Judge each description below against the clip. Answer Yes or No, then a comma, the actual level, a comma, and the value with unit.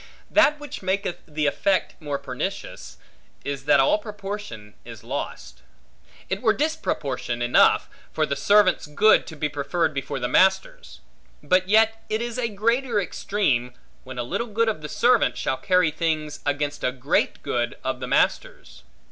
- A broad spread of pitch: Yes, wide, 7.6 semitones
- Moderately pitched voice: Yes, medium, 175 Hz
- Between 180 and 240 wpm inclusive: No, average, 160 wpm